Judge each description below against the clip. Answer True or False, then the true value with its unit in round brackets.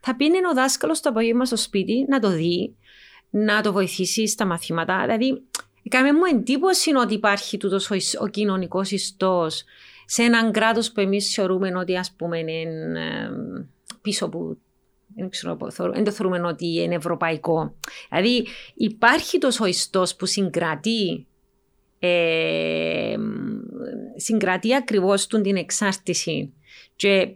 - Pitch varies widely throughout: False (4.4 semitones)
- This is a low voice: False (200 Hz)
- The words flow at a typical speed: True (125 wpm)